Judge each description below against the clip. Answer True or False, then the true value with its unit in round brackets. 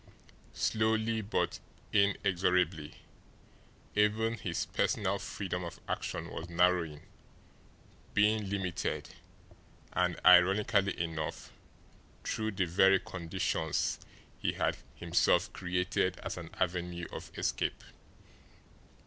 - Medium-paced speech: False (90 wpm)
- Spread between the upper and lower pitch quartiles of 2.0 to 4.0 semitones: True (2.6 semitones)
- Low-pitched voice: True (90 Hz)